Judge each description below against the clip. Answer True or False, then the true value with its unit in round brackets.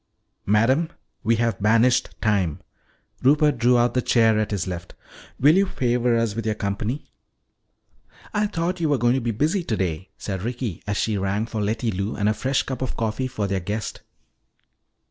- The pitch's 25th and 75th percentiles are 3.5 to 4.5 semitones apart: True (3.9 semitones)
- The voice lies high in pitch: False (115 Hz)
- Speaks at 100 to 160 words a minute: False (185 wpm)